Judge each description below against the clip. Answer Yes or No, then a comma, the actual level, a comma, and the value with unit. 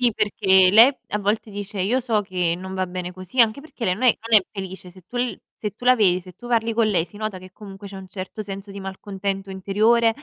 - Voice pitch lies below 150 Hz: No, high, 200 Hz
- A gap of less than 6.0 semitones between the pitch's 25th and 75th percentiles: Yes, average, 2.9 semitones